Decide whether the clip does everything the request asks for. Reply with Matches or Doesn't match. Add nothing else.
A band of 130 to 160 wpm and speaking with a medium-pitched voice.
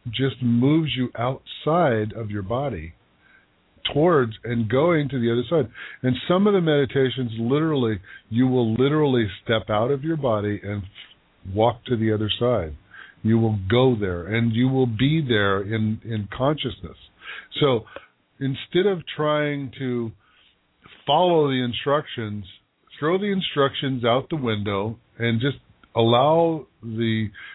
Doesn't match